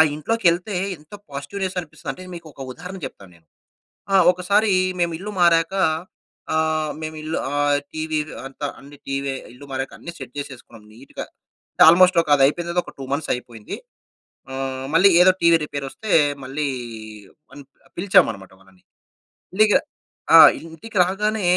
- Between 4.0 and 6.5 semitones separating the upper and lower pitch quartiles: Yes, average, 4.7 semitones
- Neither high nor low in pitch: Yes, medium, 155 Hz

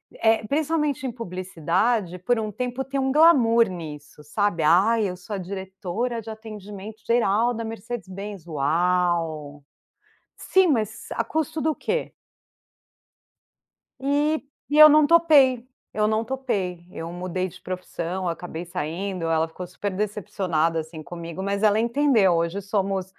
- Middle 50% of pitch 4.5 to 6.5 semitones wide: Yes, average, 5.2 semitones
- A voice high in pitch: Yes, high, 200 Hz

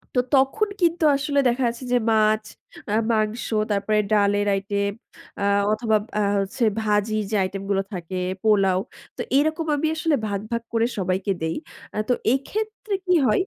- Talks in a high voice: Yes, high, 215 Hz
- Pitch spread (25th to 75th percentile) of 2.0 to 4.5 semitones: No, average, 5.2 semitones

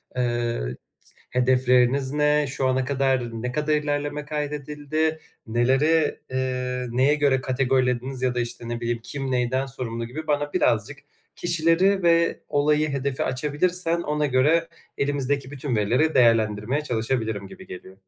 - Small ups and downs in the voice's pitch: No, average, 3.1 semitones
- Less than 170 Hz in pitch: Yes, low, 135 Hz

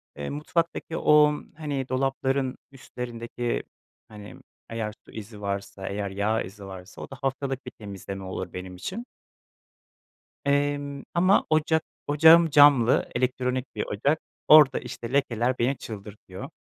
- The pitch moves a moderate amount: No, wide, 5.7 semitones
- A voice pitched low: Yes, low, 125 Hz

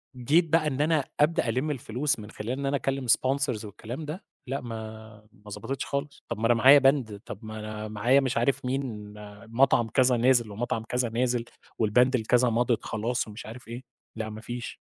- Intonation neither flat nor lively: Yes, average, 3.5 semitones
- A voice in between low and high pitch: No, low, 120 Hz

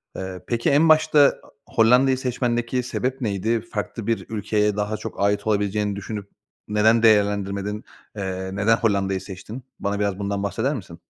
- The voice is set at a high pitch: No, low, 105 Hz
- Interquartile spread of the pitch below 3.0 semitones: Yes, narrow, 2.6 semitones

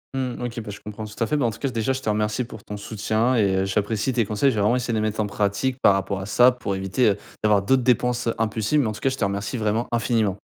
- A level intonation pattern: No, average, 3.0 semitones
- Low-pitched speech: Yes, low, 110 Hz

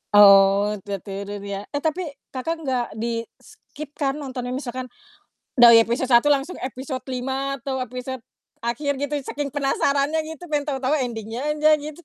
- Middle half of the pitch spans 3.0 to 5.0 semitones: Yes, average, 3.5 semitones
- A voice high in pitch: Yes, very high, 260 Hz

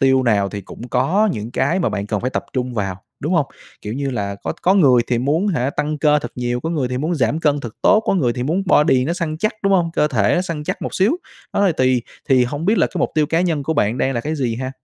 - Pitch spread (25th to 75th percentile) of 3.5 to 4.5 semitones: No, average, 5.1 semitones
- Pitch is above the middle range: No, medium, 140 Hz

